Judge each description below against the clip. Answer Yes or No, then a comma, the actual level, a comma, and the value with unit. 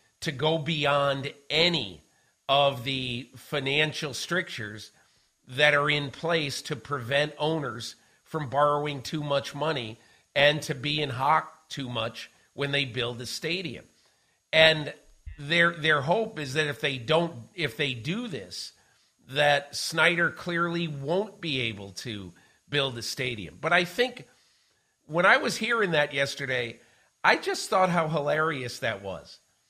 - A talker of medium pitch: Yes, medium, 145 Hz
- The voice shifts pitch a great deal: No, average, 3.5 semitones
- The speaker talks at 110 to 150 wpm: Yes, average, 145 wpm